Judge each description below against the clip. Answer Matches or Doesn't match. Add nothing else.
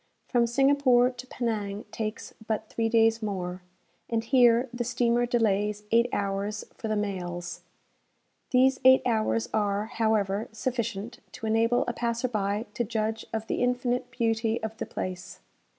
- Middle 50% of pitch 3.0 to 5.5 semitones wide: Doesn't match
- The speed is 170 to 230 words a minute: Doesn't match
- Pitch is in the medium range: Doesn't match